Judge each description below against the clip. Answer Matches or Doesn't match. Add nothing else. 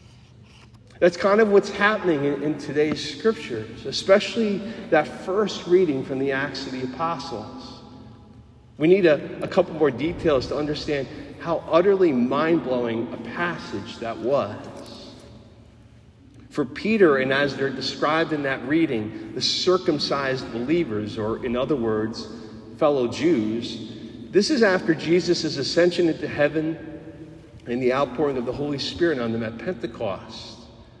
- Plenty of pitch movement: Matches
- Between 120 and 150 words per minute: Matches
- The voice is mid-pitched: Matches